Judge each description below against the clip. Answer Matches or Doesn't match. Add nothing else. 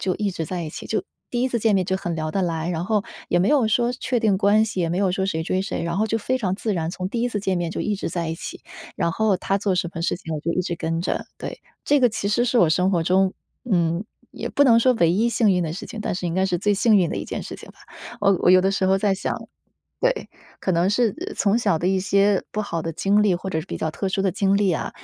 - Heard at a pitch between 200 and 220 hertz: Doesn't match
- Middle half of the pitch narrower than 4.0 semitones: Matches